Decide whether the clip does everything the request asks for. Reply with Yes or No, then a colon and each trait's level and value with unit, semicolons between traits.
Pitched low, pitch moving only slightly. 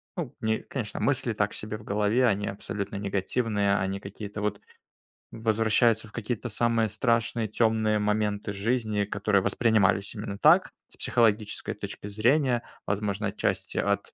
Yes: low, 105 Hz; narrow, 2.1 semitones